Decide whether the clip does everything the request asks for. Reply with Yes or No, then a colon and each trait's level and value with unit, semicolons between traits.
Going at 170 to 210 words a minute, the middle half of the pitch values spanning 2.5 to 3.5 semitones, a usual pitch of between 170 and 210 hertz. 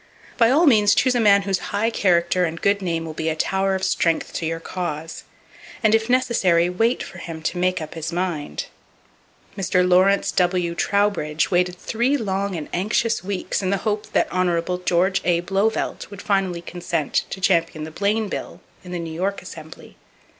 Yes: average, 185 wpm; average, 3.0 semitones; medium, 185 Hz